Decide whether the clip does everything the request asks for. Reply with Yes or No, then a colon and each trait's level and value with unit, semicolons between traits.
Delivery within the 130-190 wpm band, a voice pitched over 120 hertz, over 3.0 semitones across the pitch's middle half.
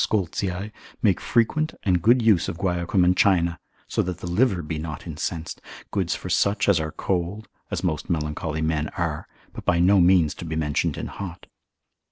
No: average, 185 wpm; very low, 90 Hz; average, 3.5 semitones